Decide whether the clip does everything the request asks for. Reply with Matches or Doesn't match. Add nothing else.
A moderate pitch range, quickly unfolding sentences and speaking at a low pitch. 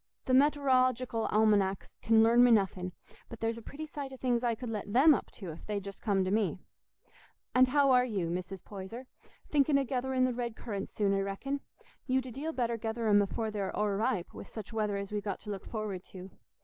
Doesn't match